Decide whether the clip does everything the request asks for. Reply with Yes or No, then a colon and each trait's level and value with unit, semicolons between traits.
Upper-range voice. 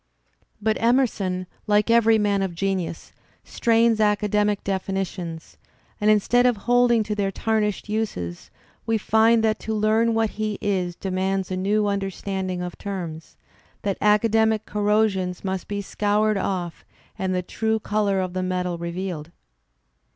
Yes: high, 205 Hz